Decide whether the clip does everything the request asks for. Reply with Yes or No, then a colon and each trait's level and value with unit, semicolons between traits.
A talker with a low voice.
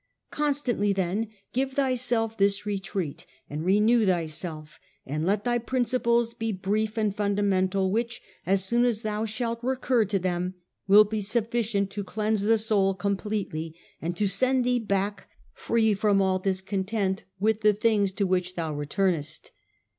No: high, 205 Hz